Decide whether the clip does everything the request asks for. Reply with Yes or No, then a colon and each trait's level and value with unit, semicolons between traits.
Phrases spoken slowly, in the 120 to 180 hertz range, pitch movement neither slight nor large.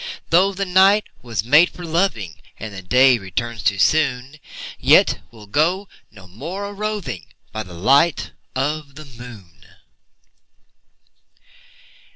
No: slow, 130 wpm; low, 135 Hz; wide, 8.4 semitones